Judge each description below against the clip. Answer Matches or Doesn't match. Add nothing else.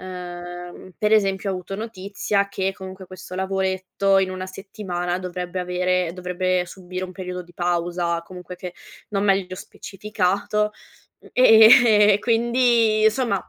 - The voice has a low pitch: Doesn't match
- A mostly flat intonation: Matches